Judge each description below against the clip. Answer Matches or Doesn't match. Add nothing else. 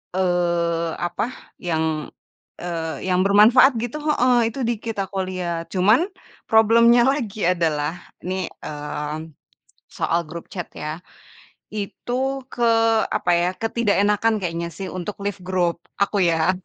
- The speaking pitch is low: Doesn't match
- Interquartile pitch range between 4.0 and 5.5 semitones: Matches